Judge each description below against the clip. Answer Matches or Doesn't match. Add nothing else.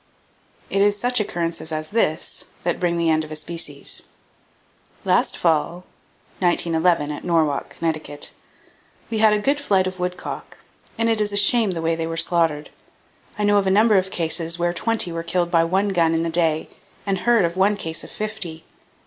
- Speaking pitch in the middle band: Matches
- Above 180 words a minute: Matches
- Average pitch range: Matches